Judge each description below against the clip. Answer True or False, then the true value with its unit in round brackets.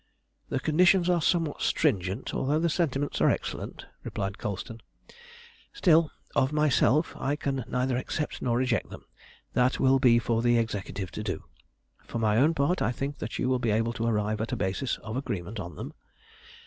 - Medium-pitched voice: False (125 Hz)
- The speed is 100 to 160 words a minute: False (180 wpm)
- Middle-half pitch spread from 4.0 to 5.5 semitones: True (4.8 semitones)